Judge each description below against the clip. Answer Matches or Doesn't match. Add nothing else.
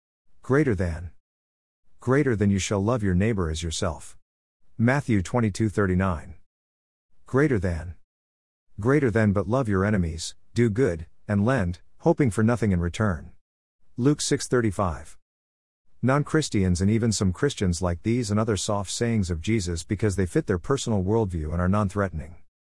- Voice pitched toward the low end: Matches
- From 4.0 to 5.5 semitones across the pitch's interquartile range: Matches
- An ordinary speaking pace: Matches